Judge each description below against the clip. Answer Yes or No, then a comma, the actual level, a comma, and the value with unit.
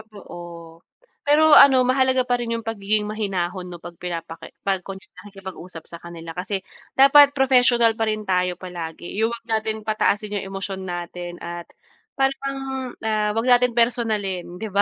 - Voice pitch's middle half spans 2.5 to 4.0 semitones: No, average, 5.0 semitones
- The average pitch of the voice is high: Yes, high, 210 Hz